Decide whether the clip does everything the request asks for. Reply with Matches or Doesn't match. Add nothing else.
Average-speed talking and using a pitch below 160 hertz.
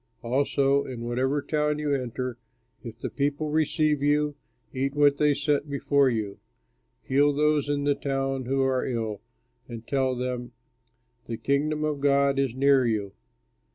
Matches